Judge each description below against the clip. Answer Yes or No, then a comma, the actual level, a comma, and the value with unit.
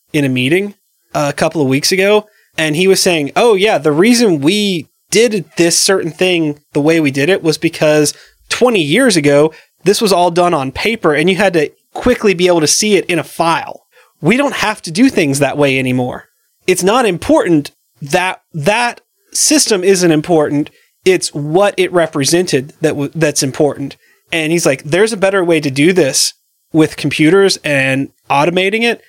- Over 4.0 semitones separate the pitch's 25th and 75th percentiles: Yes, average, 4.9 semitones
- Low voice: No, medium, 170 Hz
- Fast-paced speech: No, average, 185 wpm